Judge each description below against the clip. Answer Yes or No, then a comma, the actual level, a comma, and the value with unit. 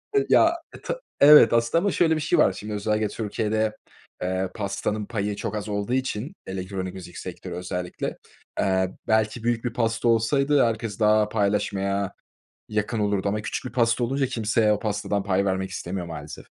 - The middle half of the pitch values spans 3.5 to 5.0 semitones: No, average, 2.9 semitones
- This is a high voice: No, low, 105 Hz